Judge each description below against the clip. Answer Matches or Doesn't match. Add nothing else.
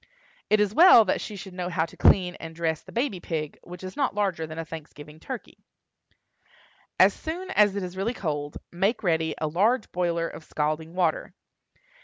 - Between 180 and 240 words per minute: Matches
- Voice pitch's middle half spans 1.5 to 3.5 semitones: Doesn't match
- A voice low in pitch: Doesn't match